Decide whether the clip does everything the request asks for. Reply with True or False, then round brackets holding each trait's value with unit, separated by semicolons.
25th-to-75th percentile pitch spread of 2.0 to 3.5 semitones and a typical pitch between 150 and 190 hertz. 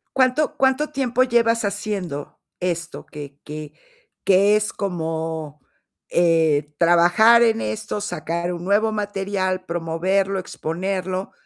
False (4.4 semitones; 185 Hz)